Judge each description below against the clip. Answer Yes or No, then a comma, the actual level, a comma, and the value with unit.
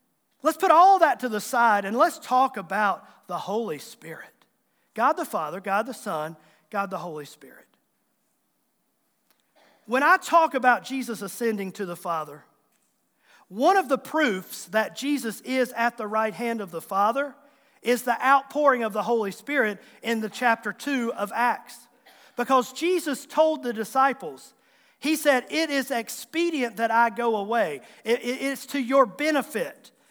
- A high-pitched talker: Yes, high, 235 Hz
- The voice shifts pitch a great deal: No, average, 4.8 semitones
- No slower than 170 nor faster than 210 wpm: No, average, 160 wpm